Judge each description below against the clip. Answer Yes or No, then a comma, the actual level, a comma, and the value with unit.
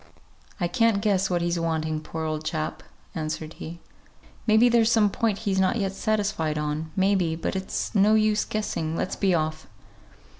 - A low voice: No, medium, 185 Hz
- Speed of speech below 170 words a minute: No, average, 180 wpm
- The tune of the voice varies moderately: Yes, average, 4.8 semitones